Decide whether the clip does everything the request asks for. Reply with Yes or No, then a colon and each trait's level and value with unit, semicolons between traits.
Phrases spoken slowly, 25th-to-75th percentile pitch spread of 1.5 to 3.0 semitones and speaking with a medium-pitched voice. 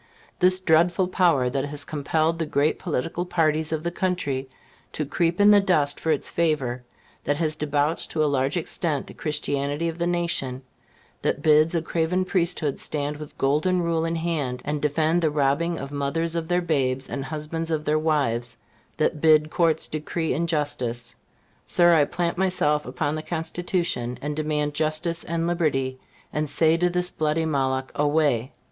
No: average, 170 wpm; narrow, 2.6 semitones; medium, 155 Hz